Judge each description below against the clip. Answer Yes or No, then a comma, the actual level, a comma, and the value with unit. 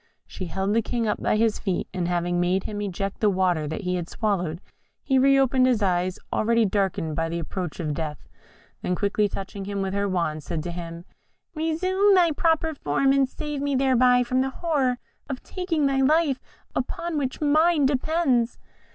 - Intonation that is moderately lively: No, wide, 7.2 semitones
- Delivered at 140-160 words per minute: No, average, 185 wpm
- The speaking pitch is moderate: No, high, 220 Hz